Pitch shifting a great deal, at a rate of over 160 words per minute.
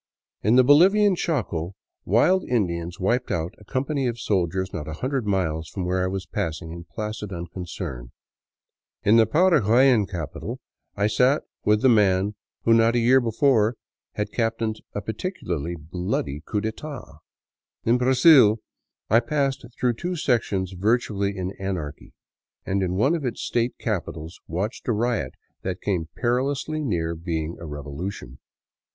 No: wide, 5.9 semitones; average, 150 wpm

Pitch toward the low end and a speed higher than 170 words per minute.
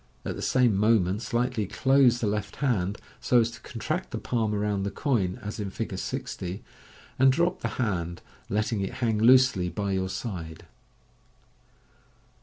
No: low, 105 Hz; average, 160 wpm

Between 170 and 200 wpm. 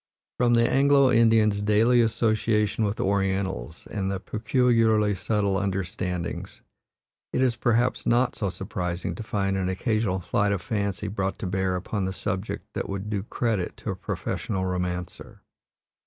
No: average, 150 wpm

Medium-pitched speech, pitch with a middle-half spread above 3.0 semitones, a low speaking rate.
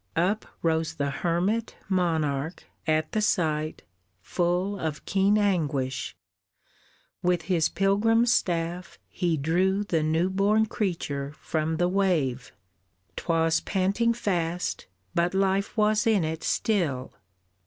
Yes: medium, 175 Hz; average, 3.7 semitones; slow, 115 wpm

